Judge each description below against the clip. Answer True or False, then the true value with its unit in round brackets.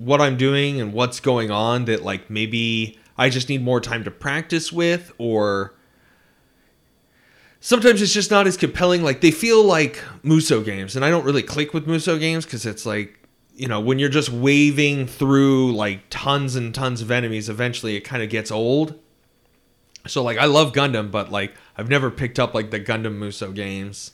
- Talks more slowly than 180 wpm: False (190 wpm)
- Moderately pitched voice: False (125 Hz)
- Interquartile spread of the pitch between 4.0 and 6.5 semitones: True (5.0 semitones)